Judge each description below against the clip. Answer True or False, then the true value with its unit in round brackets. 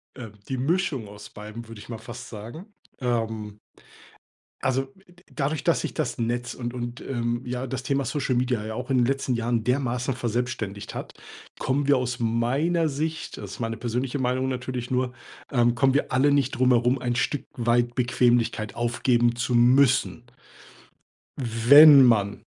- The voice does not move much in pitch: True (2.1 semitones)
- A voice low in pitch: True (125 Hz)